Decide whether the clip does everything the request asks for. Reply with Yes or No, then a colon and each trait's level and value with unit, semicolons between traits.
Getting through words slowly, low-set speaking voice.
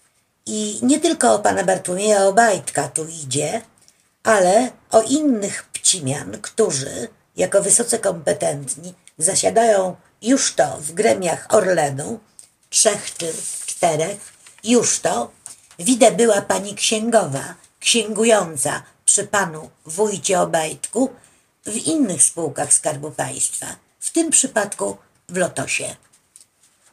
No: slow, 105 wpm; high, 200 Hz